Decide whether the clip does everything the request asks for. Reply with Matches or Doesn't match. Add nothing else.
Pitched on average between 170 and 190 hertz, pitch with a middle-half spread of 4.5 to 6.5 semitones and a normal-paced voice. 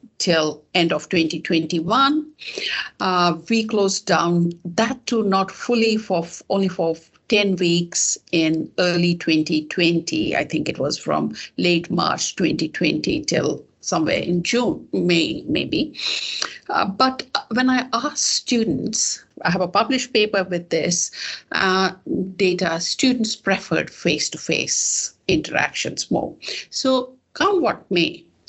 Doesn't match